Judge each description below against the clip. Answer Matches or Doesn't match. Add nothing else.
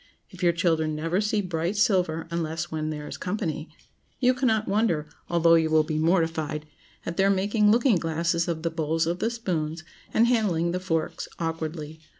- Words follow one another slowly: Doesn't match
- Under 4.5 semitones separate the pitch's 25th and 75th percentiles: Matches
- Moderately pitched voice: Matches